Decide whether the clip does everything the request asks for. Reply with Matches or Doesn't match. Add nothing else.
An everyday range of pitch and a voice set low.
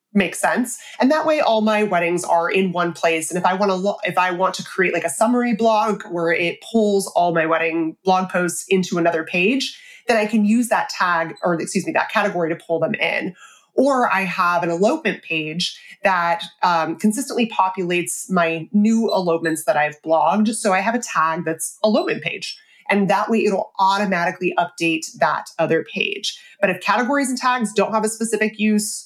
Doesn't match